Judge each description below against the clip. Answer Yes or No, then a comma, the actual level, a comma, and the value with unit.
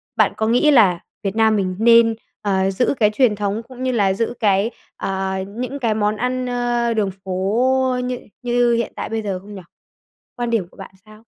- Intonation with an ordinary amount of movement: Yes, average, 3.5 semitones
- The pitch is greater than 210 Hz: Yes, high, 220 Hz